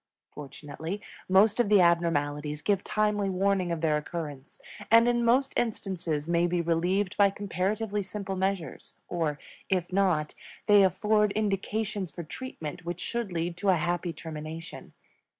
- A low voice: No, medium, 185 Hz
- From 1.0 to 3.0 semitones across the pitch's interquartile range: No, average, 3.8 semitones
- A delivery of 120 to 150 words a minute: Yes, average, 145 wpm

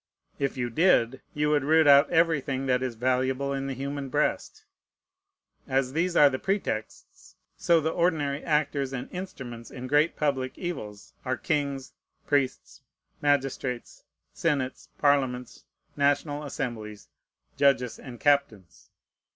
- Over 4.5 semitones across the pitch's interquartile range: No, narrow, 2.4 semitones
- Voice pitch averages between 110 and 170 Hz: Yes, medium, 140 Hz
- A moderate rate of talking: No, slow, 125 wpm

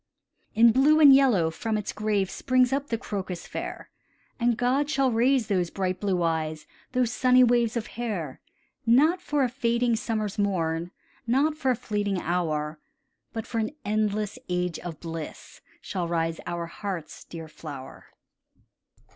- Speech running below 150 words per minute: No, average, 155 wpm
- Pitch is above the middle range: Yes, high, 215 Hz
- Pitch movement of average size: No, wide, 6.2 semitones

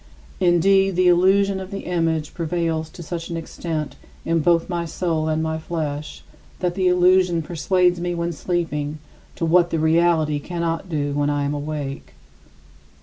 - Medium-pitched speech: Yes, medium, 170 Hz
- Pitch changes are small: Yes, narrow, 2.3 semitones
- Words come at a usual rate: Yes, average, 160 wpm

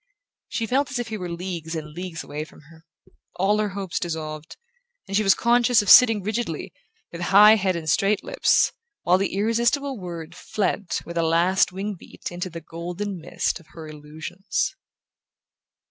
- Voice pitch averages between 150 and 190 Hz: Yes, medium, 185 Hz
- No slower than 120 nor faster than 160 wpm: No, average, 175 wpm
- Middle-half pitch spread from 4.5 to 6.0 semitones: No, average, 4.1 semitones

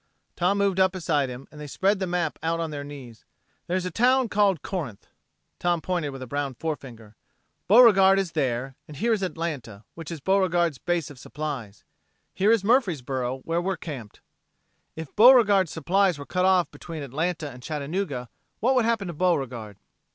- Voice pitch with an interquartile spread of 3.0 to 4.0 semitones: No, wide, 5.5 semitones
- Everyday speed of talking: Yes, average, 175 wpm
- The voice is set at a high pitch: No, medium, 165 Hz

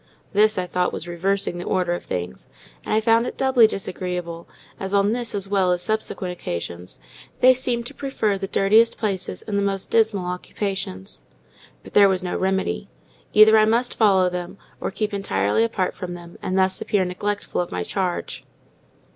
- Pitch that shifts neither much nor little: Yes, average, 3.2 semitones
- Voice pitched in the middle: No, high, 195 Hz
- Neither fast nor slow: Yes, average, 180 wpm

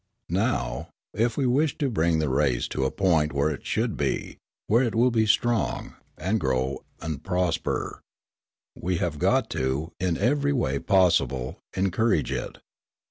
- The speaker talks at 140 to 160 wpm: Yes, average, 155 wpm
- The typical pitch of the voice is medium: No, very low, 85 Hz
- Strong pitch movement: Yes, wide, 8.1 semitones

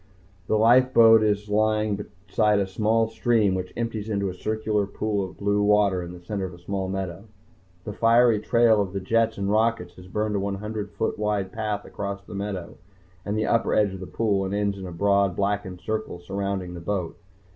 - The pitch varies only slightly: Yes, narrow, 2.0 semitones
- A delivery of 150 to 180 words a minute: No, fast, 205 wpm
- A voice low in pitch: Yes, low, 105 Hz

